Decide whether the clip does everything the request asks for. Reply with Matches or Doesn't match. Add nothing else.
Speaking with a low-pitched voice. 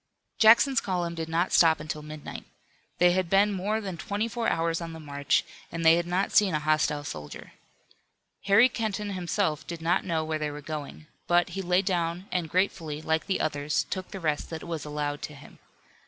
Doesn't match